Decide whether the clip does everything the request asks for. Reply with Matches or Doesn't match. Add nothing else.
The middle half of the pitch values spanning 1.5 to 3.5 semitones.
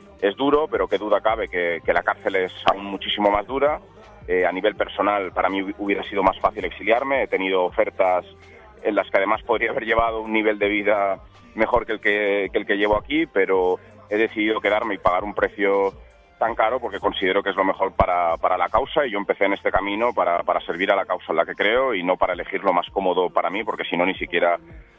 Matches